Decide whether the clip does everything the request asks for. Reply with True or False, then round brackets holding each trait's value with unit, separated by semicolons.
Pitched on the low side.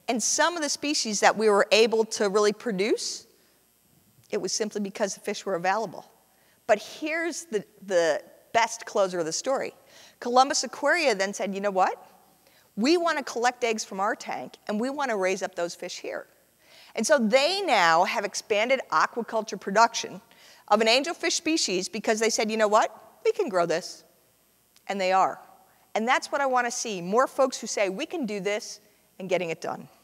False (225 Hz)